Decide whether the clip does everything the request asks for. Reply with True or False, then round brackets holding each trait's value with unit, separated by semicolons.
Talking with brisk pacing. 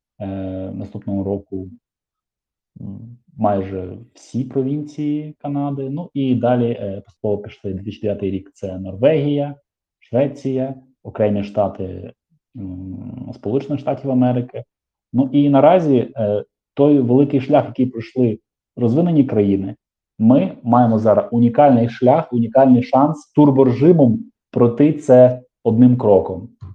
False (110 wpm)